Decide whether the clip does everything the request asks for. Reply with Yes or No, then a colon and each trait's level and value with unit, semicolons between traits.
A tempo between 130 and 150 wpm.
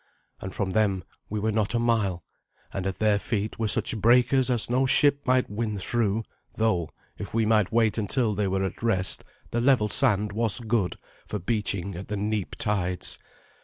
No: average, 185 wpm